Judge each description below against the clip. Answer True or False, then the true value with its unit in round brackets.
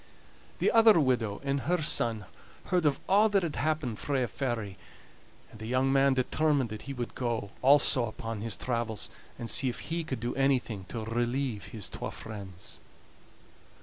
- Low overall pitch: True (125 Hz)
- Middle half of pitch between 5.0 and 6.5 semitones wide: False (4.1 semitones)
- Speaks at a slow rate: False (175 wpm)